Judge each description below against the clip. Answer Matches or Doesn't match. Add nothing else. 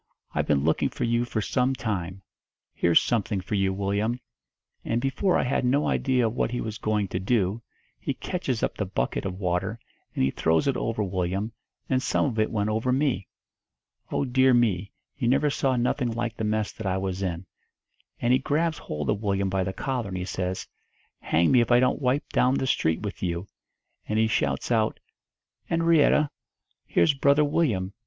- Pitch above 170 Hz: Doesn't match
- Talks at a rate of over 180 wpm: Matches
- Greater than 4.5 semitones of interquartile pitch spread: Matches